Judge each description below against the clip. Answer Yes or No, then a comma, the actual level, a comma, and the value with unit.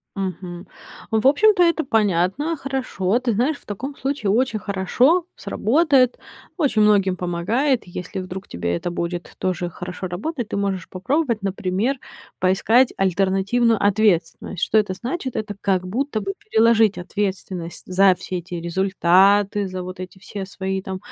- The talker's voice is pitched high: Yes, high, 200 Hz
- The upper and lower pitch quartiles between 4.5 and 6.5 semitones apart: Yes, average, 4.9 semitones